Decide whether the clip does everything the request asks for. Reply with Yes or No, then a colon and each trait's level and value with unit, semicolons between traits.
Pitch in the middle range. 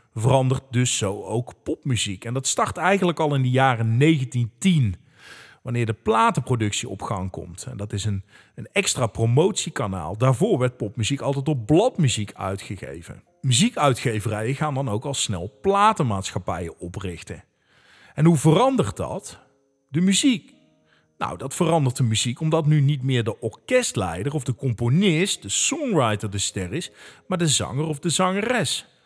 No: low, 130 Hz